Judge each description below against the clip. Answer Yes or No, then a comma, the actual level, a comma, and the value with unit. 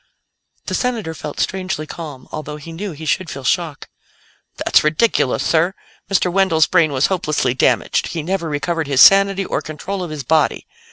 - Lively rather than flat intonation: No, average, 3.8 semitones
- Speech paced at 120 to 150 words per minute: No, average, 170 wpm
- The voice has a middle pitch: Yes, medium, 160 Hz